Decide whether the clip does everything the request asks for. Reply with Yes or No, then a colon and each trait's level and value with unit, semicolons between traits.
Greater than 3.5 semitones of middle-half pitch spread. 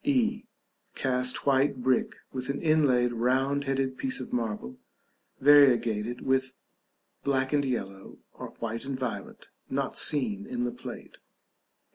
No: average, 2.9 semitones